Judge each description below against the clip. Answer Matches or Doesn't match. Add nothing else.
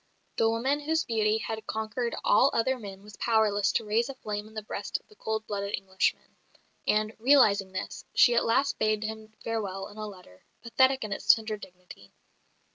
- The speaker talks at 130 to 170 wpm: Doesn't match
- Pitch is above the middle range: Matches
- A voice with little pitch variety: Matches